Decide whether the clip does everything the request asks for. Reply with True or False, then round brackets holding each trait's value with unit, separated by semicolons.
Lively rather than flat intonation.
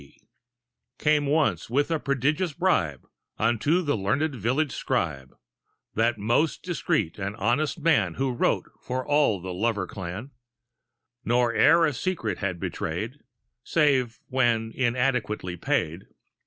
True (6.3 semitones)